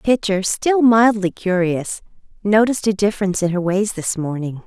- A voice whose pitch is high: Yes, high, 200 Hz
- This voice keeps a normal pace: Yes, average, 155 wpm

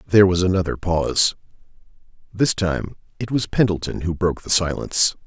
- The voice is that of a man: Yes, male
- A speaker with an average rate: Yes, average, 150 wpm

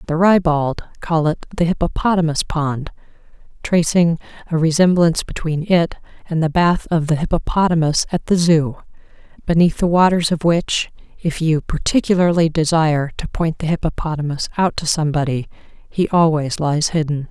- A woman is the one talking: Yes, female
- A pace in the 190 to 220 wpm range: No, average, 140 wpm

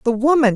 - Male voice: No, female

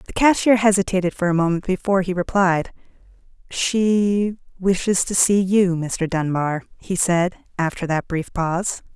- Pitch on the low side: No, medium, 185 Hz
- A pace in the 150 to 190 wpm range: No, average, 140 wpm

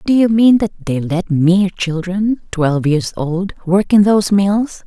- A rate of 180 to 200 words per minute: Yes, average, 185 wpm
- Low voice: No, high, 190 Hz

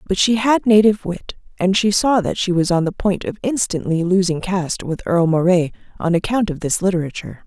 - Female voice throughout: Yes, female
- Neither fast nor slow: No, fast, 210 wpm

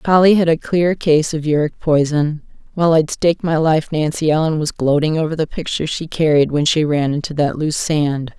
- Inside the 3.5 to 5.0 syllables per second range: No, 5.4 syllables/s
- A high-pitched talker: No, medium, 155 Hz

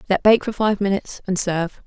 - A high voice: Yes, high, 195 Hz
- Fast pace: Yes, fast, 225 wpm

